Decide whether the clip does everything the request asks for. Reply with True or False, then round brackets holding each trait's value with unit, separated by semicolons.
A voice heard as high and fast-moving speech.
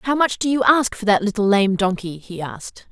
True (215 Hz; 245 wpm)